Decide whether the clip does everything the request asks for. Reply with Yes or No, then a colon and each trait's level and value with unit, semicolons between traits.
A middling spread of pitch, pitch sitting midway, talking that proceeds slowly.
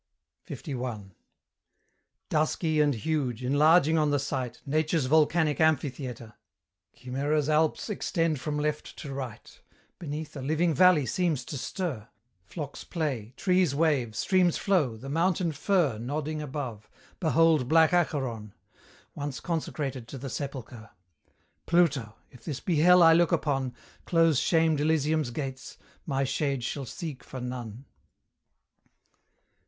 Yes: average, 3.8 semitones; medium, 145 Hz; slow, 125 wpm